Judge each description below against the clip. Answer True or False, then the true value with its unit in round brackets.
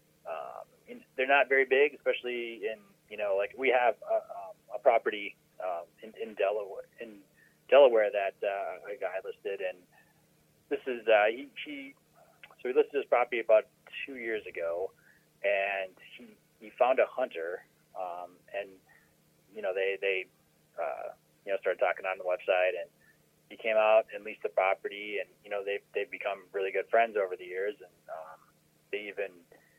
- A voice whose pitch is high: True (330 Hz)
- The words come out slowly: False (175 wpm)